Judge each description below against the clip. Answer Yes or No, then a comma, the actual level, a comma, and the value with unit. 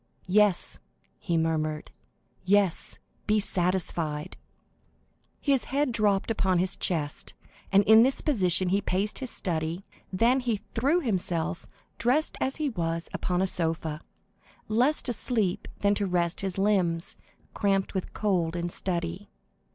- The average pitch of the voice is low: No, high, 190 Hz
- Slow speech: Yes, slow, 130 wpm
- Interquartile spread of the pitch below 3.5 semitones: No, average, 4.2 semitones